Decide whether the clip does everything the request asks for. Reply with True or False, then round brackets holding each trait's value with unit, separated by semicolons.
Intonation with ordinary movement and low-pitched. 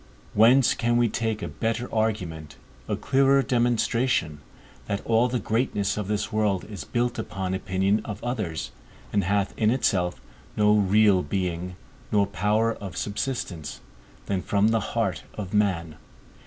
True (3.3 semitones; 105 Hz)